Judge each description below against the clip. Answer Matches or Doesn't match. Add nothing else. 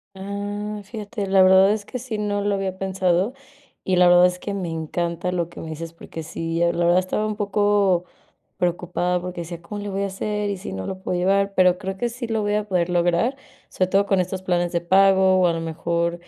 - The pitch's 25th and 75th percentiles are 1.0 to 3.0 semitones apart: Matches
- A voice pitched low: Doesn't match